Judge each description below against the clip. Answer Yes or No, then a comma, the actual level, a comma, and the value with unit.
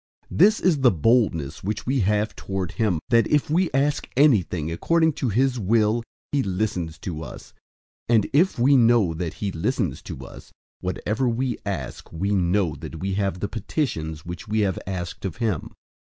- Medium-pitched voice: No, low, 105 Hz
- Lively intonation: Yes, wide, 6.0 semitones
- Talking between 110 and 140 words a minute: No, average, 180 wpm